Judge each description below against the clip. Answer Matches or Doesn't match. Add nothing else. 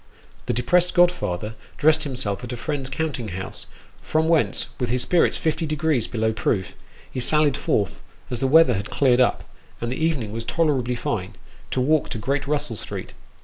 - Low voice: Matches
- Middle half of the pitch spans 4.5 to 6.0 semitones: Matches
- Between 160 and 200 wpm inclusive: Matches